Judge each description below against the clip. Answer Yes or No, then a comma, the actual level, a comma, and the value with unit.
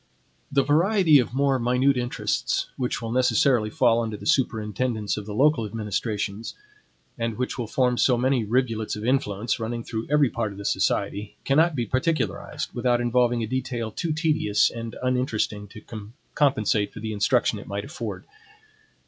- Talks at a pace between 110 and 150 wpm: No, average, 165 wpm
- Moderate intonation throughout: Yes, average, 3.4 semitones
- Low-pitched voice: Yes, low, 120 Hz